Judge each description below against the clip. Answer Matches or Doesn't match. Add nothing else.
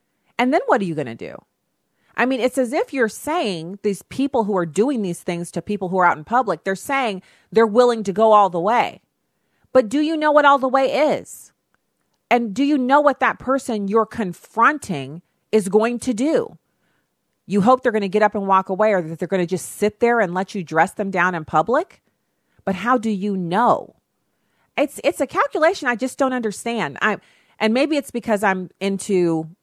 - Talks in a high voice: Matches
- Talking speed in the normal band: Doesn't match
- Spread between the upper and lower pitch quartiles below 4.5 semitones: Doesn't match